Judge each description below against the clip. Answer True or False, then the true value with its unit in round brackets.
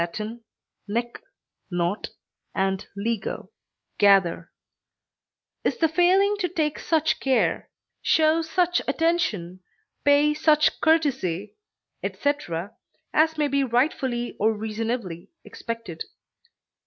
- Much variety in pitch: True (7.6 semitones)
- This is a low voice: False (255 Hz)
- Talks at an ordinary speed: False (90 wpm)